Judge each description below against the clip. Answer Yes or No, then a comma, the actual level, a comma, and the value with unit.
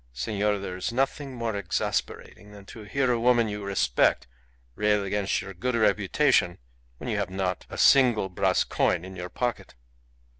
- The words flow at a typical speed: Yes, average, 165 wpm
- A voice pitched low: Yes, low, 105 Hz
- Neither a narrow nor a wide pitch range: Yes, average, 3.7 semitones